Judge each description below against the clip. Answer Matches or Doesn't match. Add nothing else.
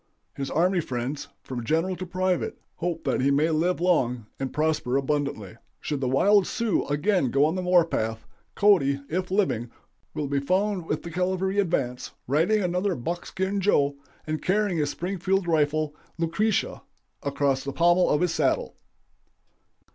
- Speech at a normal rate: Matches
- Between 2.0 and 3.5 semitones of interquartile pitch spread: Doesn't match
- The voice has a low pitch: Doesn't match